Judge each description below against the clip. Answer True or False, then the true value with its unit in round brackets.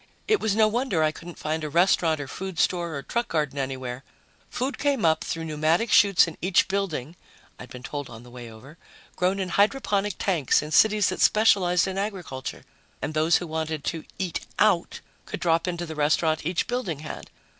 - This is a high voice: False (170 Hz)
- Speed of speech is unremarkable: True (195 wpm)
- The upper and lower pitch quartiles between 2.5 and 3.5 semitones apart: False (4.3 semitones)